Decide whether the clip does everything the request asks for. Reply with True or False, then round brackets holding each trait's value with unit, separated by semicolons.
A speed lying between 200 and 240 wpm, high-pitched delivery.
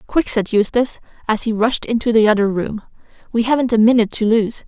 True (205 wpm; 225 Hz)